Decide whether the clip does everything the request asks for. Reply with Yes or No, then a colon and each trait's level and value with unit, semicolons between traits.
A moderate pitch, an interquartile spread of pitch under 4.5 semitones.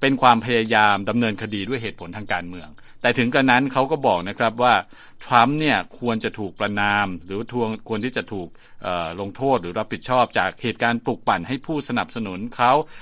No: low, 115 Hz; average, 3.4 semitones